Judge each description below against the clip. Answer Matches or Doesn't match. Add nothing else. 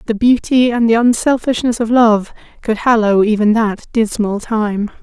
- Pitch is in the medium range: Doesn't match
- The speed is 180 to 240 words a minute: Doesn't match